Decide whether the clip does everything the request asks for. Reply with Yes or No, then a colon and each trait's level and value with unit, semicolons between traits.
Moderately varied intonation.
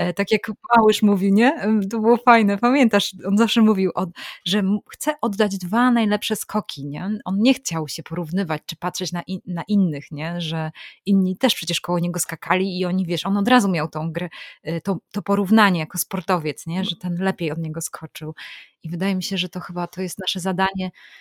Yes: average, 3.3 semitones